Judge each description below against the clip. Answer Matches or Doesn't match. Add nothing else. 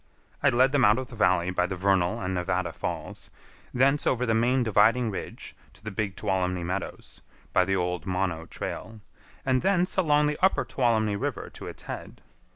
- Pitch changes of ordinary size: Doesn't match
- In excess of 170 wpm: Matches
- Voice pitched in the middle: Doesn't match